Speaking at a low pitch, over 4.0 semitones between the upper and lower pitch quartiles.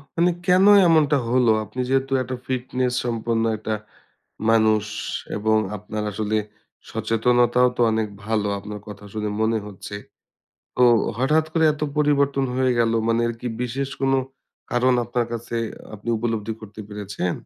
No: low, 120 Hz; average, 3.2 semitones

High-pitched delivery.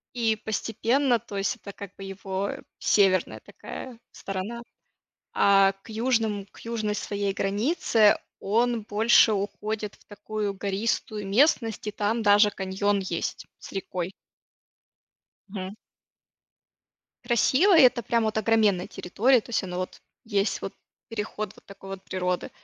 Yes: high, 210 Hz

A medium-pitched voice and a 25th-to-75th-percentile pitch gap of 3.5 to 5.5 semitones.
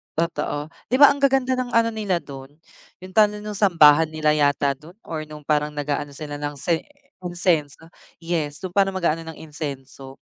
Yes: medium, 160 Hz; average, 4.3 semitones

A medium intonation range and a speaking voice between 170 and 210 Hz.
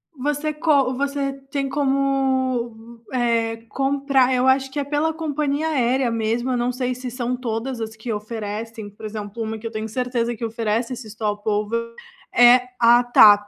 No: average, 3.1 semitones; high, 245 Hz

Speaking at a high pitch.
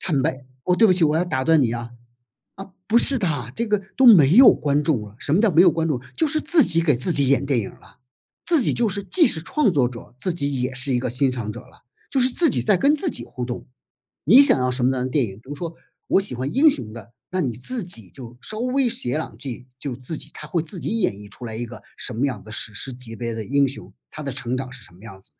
No: medium, 140 Hz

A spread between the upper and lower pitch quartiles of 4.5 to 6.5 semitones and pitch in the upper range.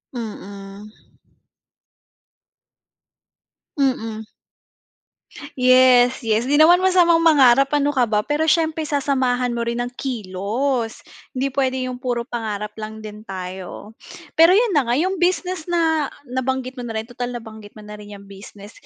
Yes: average, 5.0 semitones; high, 245 Hz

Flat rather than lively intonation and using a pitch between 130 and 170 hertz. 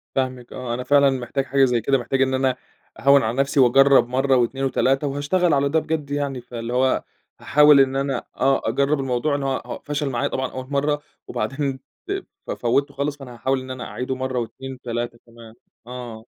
Yes: narrow, 2.0 semitones; low, 135 Hz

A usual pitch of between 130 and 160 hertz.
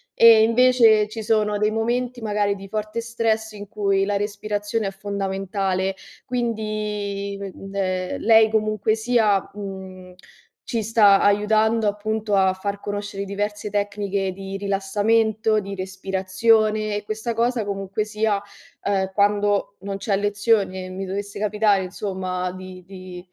No: high, 205 Hz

